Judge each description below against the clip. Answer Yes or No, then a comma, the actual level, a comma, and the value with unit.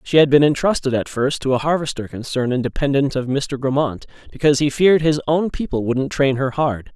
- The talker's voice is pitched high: No, medium, 140 Hz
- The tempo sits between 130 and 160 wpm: No, fast, 205 wpm